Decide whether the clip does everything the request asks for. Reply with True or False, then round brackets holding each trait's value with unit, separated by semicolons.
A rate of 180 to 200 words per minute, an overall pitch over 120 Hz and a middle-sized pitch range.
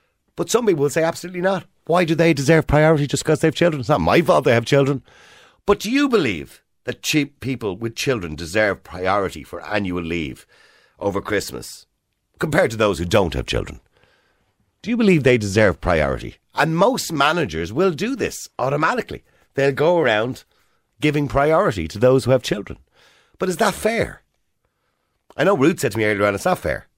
False (190 wpm; 135 Hz; 7.5 semitones)